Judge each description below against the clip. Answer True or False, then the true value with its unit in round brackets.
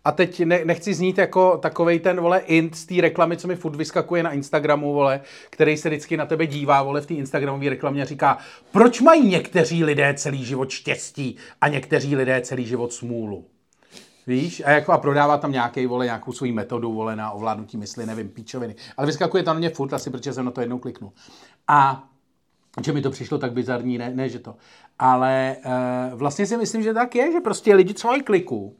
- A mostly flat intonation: False (5.0 semitones)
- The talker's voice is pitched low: False (145 Hz)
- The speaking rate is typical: False (205 wpm)